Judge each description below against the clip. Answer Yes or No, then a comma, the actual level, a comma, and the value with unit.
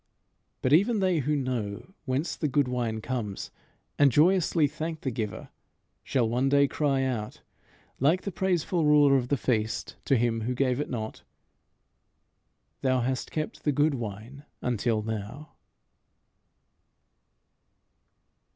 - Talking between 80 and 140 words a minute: Yes, slow, 135 wpm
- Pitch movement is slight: No, average, 4.0 semitones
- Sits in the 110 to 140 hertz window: Yes, low, 135 Hz